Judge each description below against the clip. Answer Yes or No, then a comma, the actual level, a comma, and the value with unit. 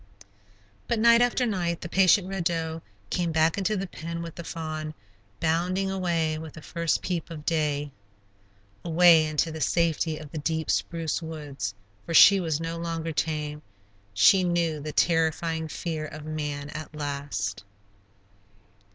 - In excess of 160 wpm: No, average, 150 wpm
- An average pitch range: No, narrow, 1.9 semitones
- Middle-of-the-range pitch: Yes, medium, 160 Hz